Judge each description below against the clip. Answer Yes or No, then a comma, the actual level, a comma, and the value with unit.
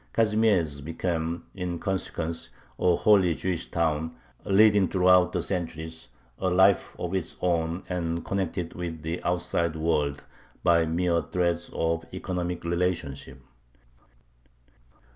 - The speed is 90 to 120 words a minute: Yes, slow, 115 wpm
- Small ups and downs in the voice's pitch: Yes, narrow, 2.0 semitones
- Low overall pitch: Yes, very low, 85 Hz